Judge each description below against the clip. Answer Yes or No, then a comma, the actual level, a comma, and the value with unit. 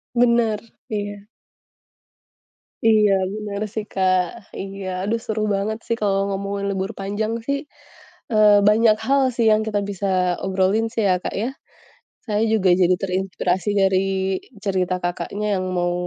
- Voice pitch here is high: Yes, high, 205 Hz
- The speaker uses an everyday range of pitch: No, narrow, 2.1 semitones